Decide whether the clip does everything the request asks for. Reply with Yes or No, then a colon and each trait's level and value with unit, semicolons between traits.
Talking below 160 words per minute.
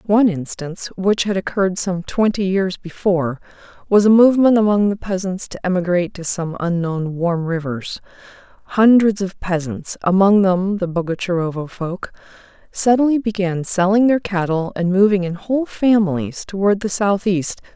Yes: average, 145 wpm